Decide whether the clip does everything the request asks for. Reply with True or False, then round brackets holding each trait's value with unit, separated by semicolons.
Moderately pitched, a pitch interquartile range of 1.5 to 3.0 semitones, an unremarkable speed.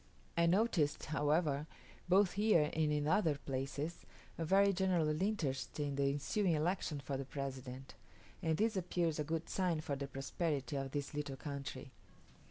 False (150 Hz; 3.8 semitones; 160 wpm)